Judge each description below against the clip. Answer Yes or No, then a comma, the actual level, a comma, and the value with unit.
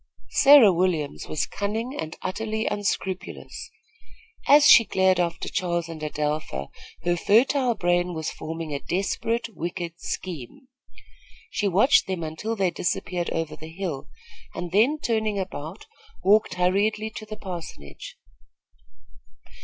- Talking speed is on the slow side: Yes, slow, 125 wpm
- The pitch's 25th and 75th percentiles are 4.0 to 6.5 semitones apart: Yes, average, 4.6 semitones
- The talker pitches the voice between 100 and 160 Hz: No, medium, 185 Hz